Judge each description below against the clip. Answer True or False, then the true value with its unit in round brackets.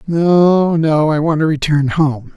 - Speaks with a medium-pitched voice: True (155 Hz)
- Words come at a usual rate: True (180 wpm)